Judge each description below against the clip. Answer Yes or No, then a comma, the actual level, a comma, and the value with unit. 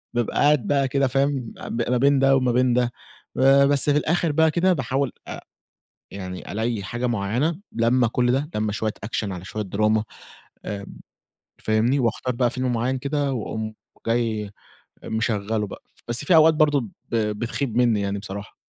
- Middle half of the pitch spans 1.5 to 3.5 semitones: No, average, 4.1 semitones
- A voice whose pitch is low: Yes, low, 120 Hz